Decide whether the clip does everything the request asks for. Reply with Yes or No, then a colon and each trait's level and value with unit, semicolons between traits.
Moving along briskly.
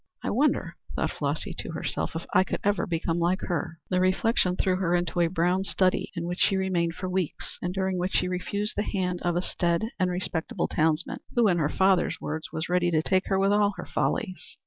Yes: fast, 220 wpm